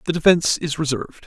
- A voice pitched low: No, medium, 155 Hz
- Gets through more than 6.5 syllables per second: Yes, 7.1 syllables/s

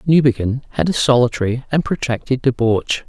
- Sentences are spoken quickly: No, slow, 135 wpm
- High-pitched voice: No, low, 130 Hz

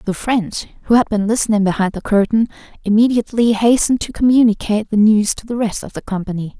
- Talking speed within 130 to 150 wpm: No, average, 190 wpm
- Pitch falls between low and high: No, high, 215 Hz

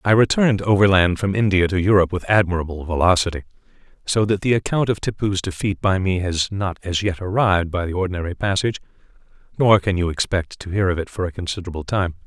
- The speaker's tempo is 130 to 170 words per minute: No, average, 195 wpm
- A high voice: No, very low, 95 Hz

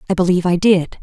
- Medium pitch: Yes, medium, 180 Hz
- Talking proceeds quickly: Yes, fast, 235 wpm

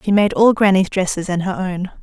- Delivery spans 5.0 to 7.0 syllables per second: Yes, 5.5 syllables/s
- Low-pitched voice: No, high, 190 Hz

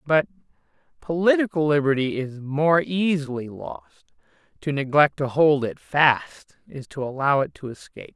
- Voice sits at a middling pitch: Yes, medium, 150 Hz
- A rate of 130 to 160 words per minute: Yes, average, 140 wpm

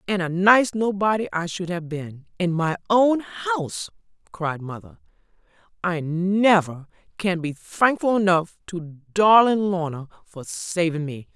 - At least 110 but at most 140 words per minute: Yes, slow, 135 wpm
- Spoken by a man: No, female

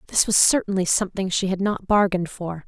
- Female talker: Yes, female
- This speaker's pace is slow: No, average, 200 wpm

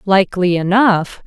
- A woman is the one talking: Yes, female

